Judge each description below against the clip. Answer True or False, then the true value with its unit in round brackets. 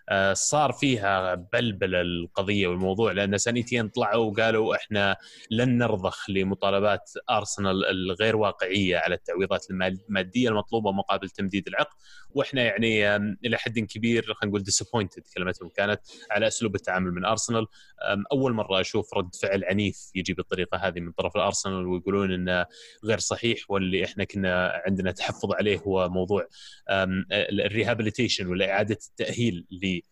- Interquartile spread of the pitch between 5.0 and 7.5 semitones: False (3.1 semitones)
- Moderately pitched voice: False (100 Hz)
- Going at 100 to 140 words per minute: True (135 wpm)